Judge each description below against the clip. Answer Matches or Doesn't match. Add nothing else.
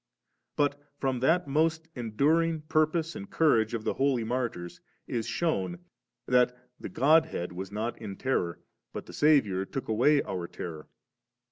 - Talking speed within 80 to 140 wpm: Doesn't match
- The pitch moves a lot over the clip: Matches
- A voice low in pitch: Matches